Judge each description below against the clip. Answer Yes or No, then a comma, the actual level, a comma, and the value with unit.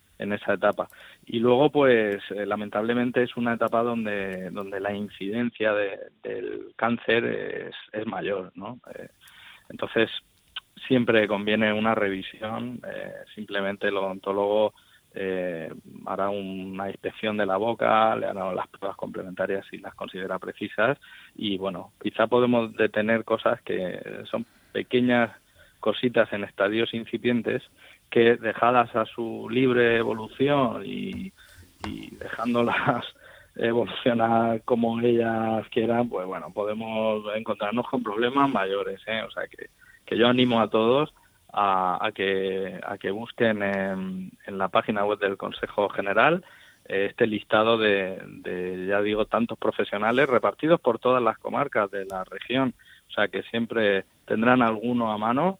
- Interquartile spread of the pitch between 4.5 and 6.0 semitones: No, average, 3.1 semitones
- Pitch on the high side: No, low, 110 Hz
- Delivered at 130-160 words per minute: Yes, average, 140 wpm